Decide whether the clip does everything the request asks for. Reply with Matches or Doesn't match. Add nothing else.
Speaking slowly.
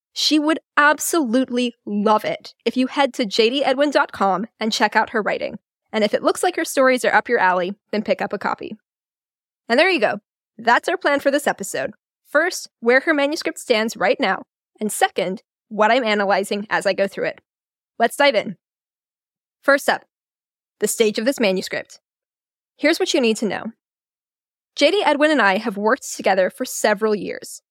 Doesn't match